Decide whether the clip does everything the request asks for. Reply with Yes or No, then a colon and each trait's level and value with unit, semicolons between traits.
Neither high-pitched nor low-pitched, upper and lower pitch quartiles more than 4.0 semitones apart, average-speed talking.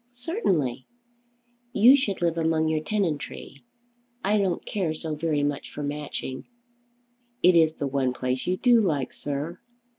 Yes: medium, 160 Hz; average, 4.9 semitones; average, 145 wpm